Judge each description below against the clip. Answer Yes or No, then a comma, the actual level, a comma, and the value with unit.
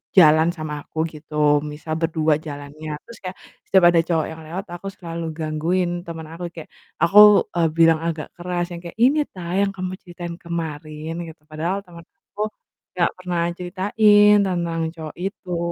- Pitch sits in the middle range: Yes, medium, 170 Hz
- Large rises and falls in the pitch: No, narrow, 2.4 semitones